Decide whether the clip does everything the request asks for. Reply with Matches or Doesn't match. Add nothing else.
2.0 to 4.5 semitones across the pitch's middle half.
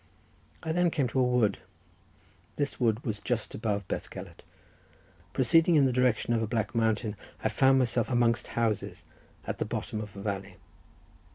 Matches